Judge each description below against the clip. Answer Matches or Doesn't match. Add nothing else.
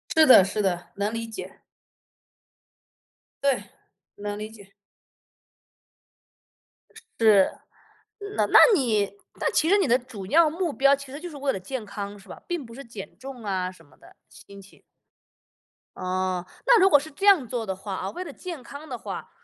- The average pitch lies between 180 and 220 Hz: Doesn't match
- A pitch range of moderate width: Doesn't match